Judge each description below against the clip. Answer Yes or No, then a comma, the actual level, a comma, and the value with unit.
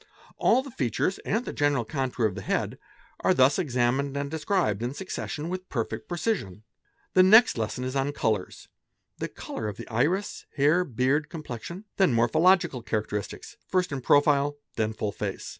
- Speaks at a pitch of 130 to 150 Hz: Yes, medium, 140 Hz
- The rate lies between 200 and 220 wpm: No, average, 170 wpm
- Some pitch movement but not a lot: No, wide, 6.8 semitones